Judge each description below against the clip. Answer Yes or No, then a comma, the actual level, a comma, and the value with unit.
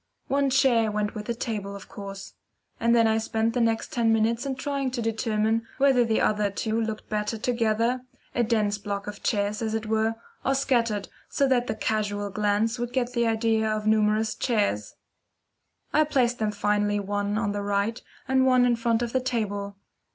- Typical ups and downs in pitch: No, narrow, 2.3 semitones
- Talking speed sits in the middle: Yes, average, 190 wpm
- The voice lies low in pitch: No, high, 225 Hz